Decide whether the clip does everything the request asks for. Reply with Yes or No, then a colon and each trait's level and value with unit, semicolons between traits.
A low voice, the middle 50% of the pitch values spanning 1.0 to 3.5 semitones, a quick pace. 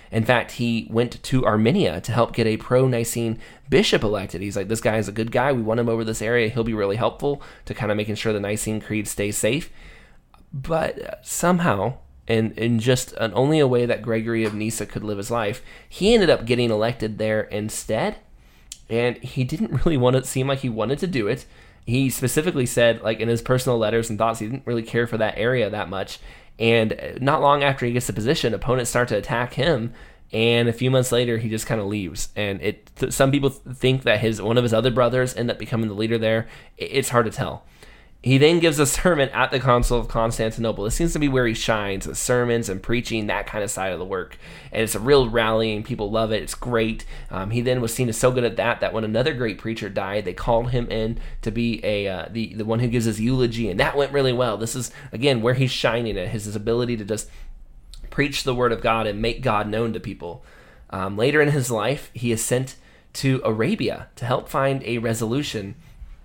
Yes: low, 115 Hz; average, 2.7 semitones; fast, 235 wpm